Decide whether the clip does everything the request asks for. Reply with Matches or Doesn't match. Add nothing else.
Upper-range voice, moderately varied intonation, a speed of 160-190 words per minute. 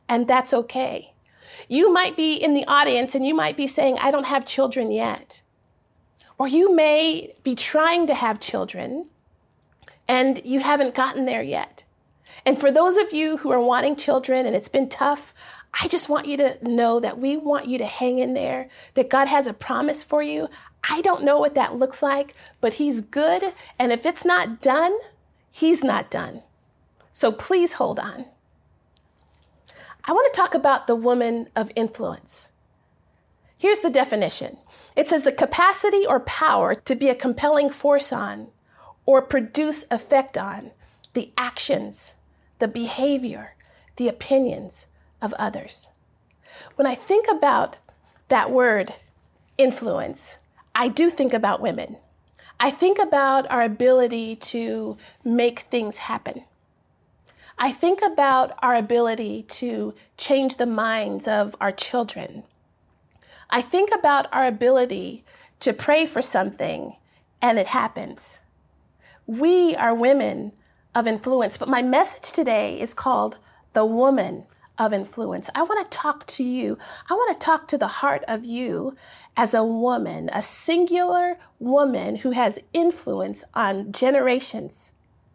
Doesn't match